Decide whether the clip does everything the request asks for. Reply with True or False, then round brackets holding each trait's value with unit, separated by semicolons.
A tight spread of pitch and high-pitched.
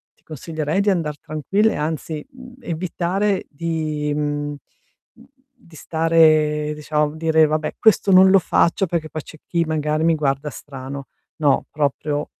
False (2.1 semitones; 155 Hz)